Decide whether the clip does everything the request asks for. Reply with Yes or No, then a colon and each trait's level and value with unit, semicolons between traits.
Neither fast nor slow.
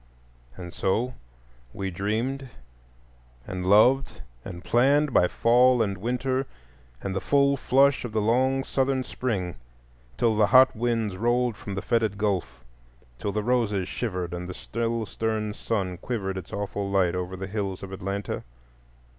Yes: average, 150 wpm